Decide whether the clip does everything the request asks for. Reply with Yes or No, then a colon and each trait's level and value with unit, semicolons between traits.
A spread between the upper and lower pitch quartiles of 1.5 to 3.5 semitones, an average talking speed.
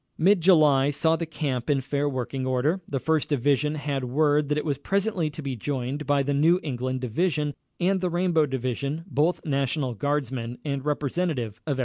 Yes: average, 3.1 semitones; average, 195 wpm